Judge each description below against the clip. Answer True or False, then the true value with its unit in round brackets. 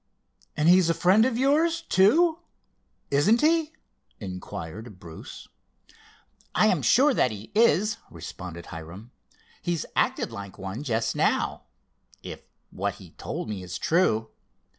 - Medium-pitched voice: True (155 Hz)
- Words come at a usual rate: False (130 wpm)